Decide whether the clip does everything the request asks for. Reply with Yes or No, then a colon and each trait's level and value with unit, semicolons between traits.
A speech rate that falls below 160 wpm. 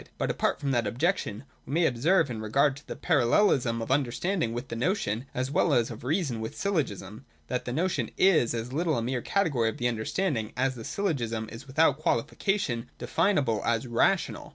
No: average, 190 wpm